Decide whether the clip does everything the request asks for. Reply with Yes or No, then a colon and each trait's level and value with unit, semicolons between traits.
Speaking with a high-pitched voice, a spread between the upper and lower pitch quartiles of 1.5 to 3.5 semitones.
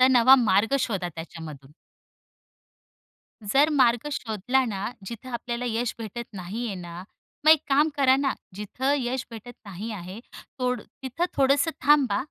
No: high, 235 Hz; average, 4.8 semitones